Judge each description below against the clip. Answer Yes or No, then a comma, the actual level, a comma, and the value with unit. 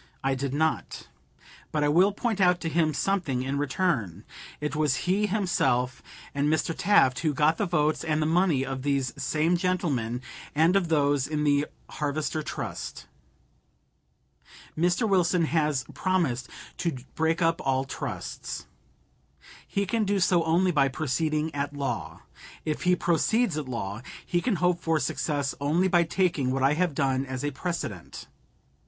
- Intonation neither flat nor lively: Yes, average, 4.2 semitones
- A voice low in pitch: No, medium, 155 Hz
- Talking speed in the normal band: Yes, average, 160 wpm